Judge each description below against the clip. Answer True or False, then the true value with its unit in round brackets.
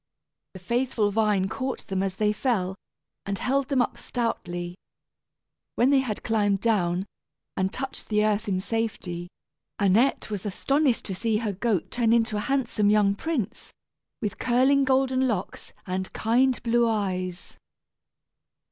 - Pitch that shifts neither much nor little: True (4.2 semitones)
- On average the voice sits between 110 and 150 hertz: False (215 Hz)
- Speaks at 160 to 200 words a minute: False (145 wpm)